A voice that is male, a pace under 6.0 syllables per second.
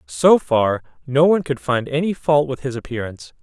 Yes: male; 5.4 syllables/s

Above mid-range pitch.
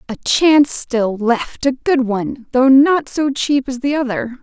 Yes: very high, 260 Hz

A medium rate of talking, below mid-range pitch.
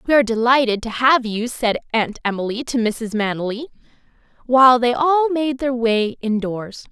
No: average, 165 wpm; high, 240 Hz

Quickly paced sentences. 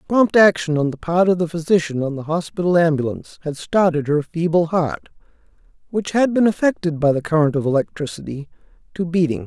No: average, 175 wpm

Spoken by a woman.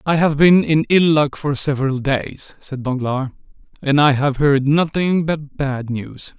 No: male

